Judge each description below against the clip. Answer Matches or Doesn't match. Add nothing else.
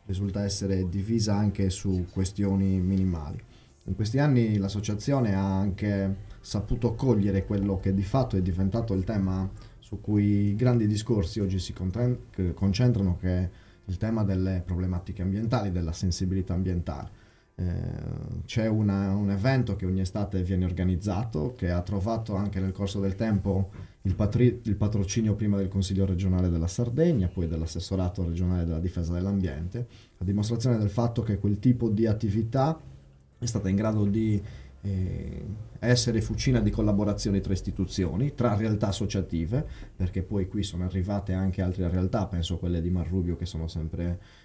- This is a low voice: Matches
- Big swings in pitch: Doesn't match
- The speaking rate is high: Doesn't match